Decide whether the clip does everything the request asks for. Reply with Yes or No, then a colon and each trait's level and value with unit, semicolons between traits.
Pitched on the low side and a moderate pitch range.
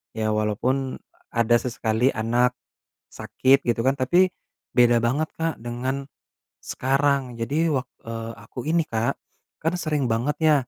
Yes: low, 125 Hz; average, 3.5 semitones